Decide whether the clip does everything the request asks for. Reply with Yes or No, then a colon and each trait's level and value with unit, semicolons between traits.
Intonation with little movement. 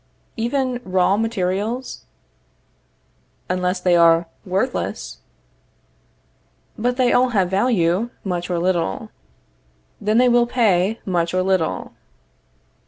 No: average, 4.8 semitones